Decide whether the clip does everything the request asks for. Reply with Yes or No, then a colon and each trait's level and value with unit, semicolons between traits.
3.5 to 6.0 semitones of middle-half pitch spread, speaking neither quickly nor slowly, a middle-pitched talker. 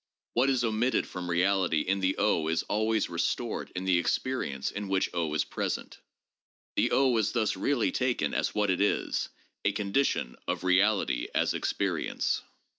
No: average, 3.9 semitones; average, 150 wpm; low, 100 Hz